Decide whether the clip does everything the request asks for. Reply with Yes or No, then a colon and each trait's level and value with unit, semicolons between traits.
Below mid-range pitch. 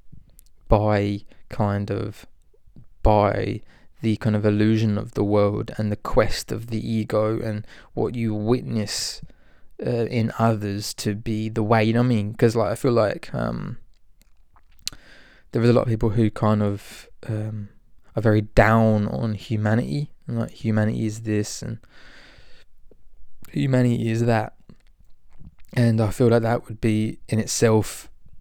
Yes: low, 110 Hz